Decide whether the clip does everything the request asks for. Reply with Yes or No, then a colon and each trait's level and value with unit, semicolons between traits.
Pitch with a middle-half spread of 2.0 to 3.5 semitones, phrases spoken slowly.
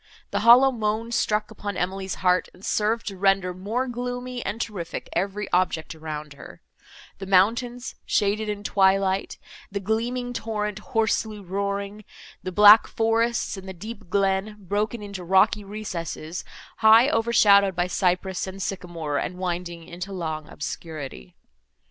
Yes: average, 3.2 semitones; slow, 130 wpm